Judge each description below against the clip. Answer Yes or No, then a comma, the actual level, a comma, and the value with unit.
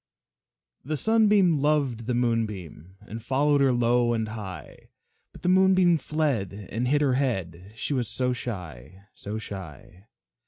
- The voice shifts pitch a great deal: Yes, wide, 6.4 semitones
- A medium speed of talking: Yes, average, 145 wpm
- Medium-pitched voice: No, low, 120 Hz